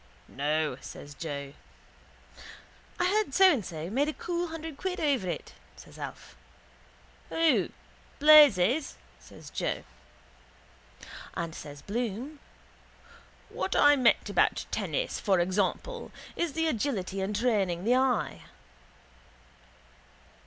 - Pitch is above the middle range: Yes, high, 245 Hz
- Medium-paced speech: No, slow, 110 wpm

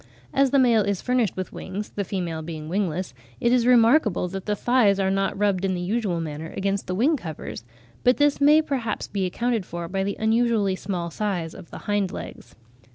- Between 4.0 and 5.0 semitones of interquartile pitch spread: Yes, average, 4.5 semitones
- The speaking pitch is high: Yes, high, 200 Hz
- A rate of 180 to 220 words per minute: Yes, fast, 205 wpm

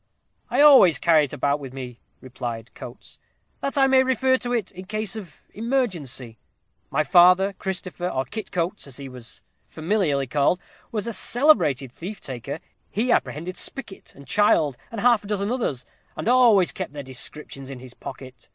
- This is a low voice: No, medium, 175 Hz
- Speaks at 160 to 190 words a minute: Yes, average, 170 wpm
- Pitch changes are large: Yes, wide, 8.2 semitones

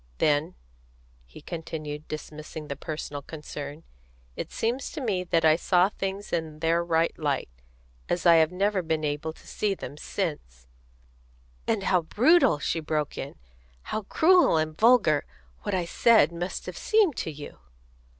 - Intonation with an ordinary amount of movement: Yes, average, 4.3 semitones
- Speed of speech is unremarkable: Yes, average, 160 wpm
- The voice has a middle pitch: Yes, medium, 160 Hz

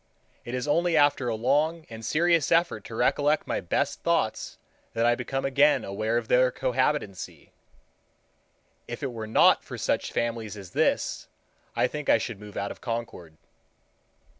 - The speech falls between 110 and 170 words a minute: Yes, average, 165 wpm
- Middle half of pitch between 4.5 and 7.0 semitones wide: Yes, average, 4.8 semitones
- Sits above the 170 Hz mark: No, low, 120 Hz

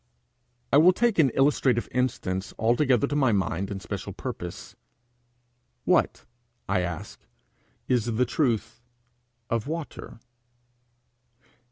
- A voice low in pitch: Yes, low, 125 Hz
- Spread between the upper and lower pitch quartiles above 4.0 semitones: Yes, wide, 5.4 semitones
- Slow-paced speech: Yes, slow, 110 wpm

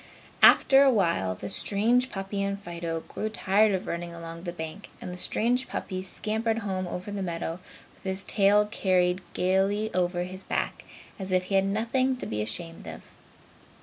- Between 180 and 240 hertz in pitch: Yes, high, 190 Hz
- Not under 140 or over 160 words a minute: No, average, 180 wpm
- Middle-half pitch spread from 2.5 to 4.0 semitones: Yes, average, 3.2 semitones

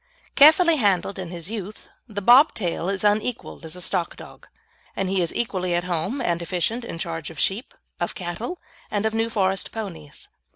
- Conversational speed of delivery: Yes, average, 190 wpm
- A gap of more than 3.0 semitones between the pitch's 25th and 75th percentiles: Yes, average, 4.5 semitones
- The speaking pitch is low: No, high, 195 Hz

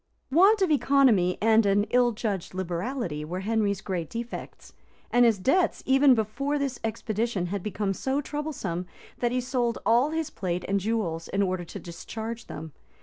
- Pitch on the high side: Yes, high, 220 Hz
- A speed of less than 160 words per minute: No, average, 165 wpm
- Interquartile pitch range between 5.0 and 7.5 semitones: Yes, wide, 5.6 semitones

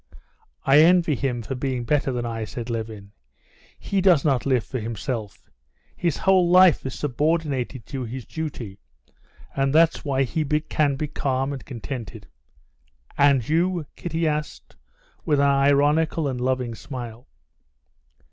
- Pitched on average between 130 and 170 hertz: Yes, low, 135 Hz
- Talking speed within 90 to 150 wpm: Yes, average, 140 wpm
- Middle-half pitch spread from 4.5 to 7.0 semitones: No, average, 4.0 semitones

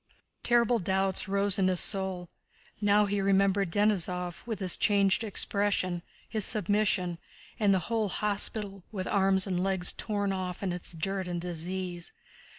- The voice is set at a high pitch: Yes, high, 195 Hz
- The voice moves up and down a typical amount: No, narrow, 2.0 semitones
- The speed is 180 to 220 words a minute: No, average, 150 wpm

